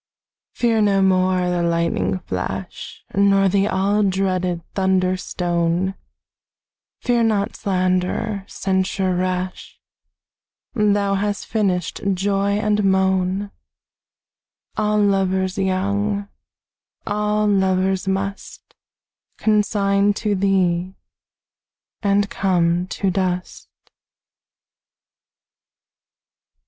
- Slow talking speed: Yes, slow, 80 wpm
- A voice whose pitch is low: No, high, 195 Hz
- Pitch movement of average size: No, narrow, 1.7 semitones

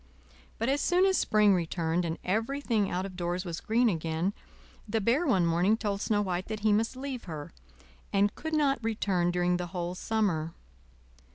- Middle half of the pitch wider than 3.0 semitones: Yes, average, 4.3 semitones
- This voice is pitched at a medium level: No, high, 200 Hz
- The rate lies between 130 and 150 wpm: No, average, 180 wpm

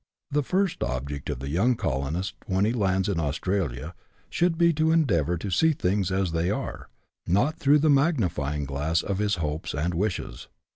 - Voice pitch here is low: Yes, very low, 95 Hz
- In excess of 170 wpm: Yes, average, 185 wpm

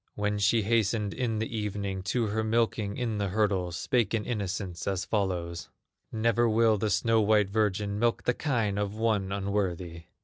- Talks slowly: No, average, 170 wpm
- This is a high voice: No, low, 105 Hz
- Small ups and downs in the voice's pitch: Yes, narrow, 2.3 semitones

